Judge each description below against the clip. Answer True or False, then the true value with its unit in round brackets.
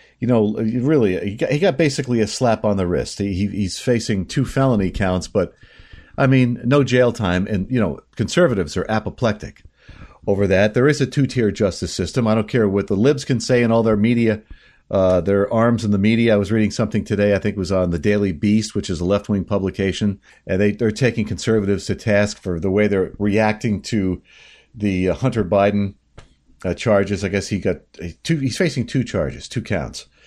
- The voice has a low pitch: True (105 Hz)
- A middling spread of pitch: True (3.0 semitones)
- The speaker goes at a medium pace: False (210 wpm)